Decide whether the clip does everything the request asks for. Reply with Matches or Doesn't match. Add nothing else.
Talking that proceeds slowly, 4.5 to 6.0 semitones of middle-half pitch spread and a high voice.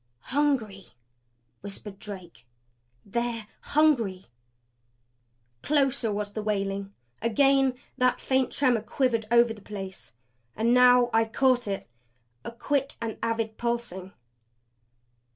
Doesn't match